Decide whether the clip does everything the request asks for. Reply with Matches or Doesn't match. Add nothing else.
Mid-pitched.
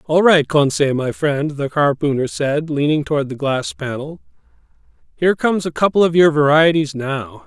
Matches